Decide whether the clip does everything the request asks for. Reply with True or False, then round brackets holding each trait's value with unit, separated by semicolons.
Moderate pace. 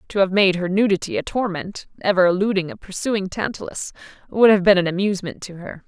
True (195 wpm)